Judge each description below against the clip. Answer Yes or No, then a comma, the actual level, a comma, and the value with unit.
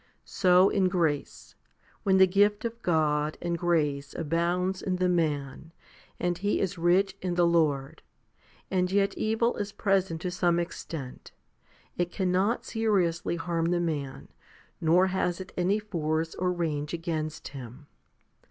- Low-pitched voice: No, medium, 175 Hz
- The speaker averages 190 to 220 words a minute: No, average, 145 wpm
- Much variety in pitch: No, average, 2.9 semitones